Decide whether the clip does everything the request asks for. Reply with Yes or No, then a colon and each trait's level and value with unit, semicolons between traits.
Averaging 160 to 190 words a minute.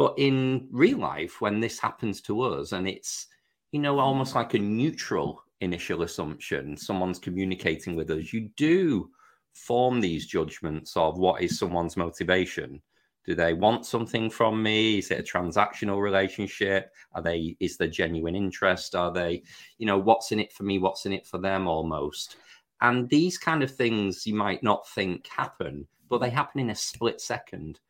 Yes: average, 175 wpm